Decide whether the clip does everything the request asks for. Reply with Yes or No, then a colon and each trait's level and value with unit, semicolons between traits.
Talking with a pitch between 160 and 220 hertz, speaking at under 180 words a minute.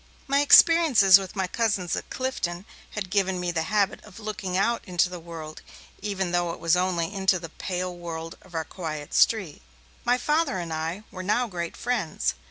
No: medium, 185 Hz; average, 185 wpm